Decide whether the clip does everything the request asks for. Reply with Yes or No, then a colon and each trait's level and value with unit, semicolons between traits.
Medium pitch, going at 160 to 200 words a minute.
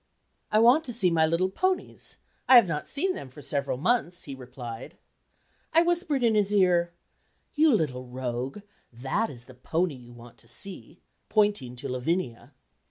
Yes: medium, 170 Hz; average, 165 wpm